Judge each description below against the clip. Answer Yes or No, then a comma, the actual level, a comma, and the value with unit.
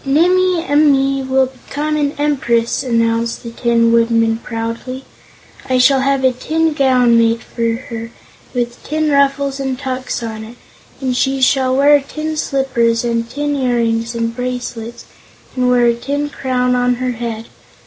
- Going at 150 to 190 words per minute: Yes, average, 155 wpm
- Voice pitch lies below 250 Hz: No, very high, 255 Hz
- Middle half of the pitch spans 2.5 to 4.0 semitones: Yes, average, 2.9 semitones